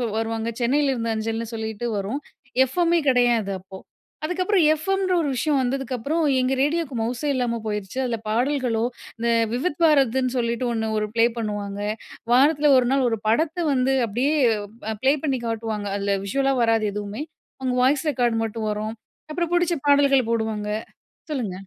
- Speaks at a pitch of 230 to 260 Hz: Yes, high, 245 Hz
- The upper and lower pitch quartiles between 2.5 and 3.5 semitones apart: No, average, 4.1 semitones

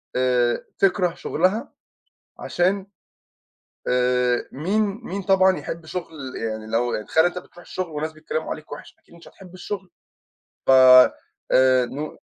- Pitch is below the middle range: No, medium, 160 Hz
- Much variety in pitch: Yes, wide, 6.5 semitones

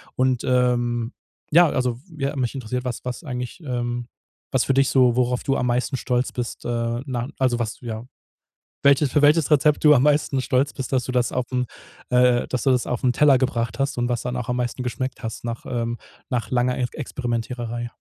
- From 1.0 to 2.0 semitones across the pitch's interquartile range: Yes, narrow, 1.6 semitones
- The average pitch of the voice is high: No, low, 125 Hz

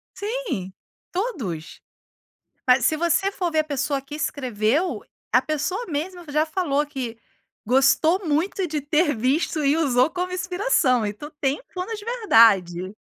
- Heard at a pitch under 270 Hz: No, very high, 300 Hz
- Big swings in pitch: Yes, wide, 6.0 semitones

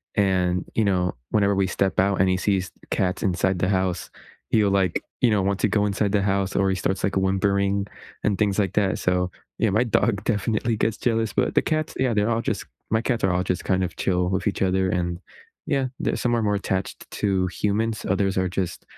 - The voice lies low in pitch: Yes, low, 100 Hz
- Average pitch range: No, narrow, 2.0 semitones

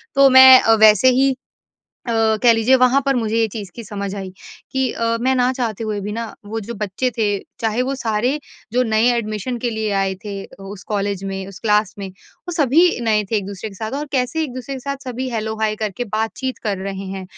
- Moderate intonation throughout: Yes, average, 3.6 semitones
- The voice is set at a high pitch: Yes, high, 225 Hz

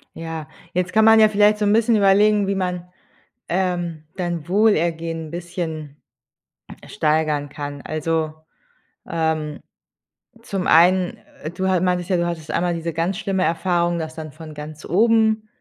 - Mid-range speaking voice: Yes, medium, 175 Hz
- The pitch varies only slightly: No, average, 3.3 semitones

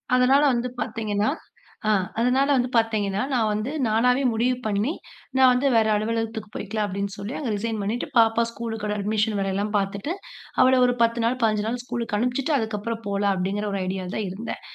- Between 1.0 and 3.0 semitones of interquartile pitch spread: Yes, average, 2.7 semitones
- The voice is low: No, high, 220 Hz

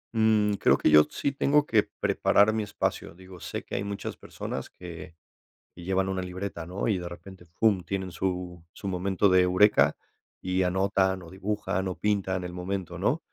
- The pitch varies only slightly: Yes, narrow, 2.0 semitones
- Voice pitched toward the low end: Yes, very low, 95 Hz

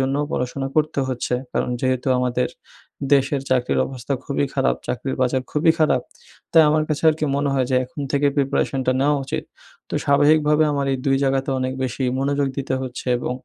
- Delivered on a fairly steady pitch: Yes, narrow, 2.0 semitones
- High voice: No, low, 135 Hz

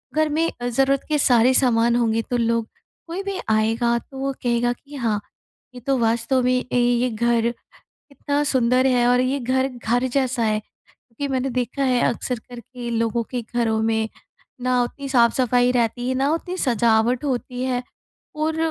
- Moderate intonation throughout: No, narrow, 2.1 semitones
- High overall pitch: Yes, high, 245 Hz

